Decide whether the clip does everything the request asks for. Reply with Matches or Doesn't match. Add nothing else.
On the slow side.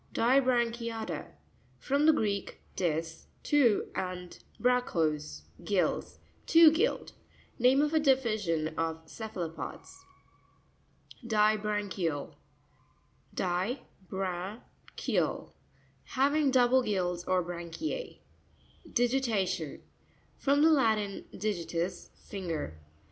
Matches